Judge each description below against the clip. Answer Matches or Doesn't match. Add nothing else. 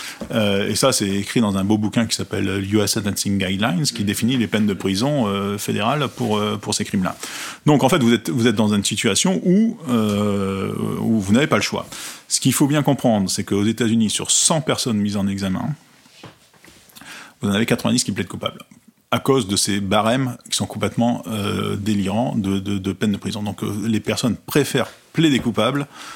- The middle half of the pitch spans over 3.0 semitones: Matches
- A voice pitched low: Matches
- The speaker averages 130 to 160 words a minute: Doesn't match